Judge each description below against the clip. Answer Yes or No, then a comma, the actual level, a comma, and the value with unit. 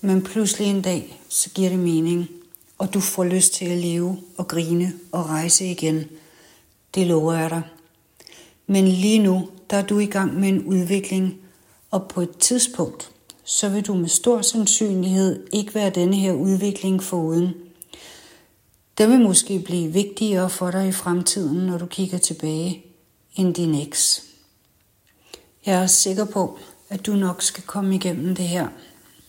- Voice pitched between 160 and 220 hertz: Yes, medium, 185 Hz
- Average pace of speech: Yes, average, 160 wpm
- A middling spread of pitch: No, narrow, 2.0 semitones